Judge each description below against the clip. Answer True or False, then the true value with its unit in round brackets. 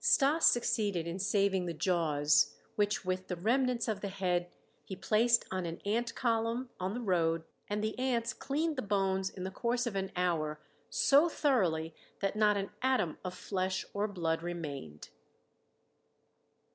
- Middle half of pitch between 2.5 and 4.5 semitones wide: False (4.9 semitones)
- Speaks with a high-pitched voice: True (195 Hz)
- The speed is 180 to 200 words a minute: False (160 wpm)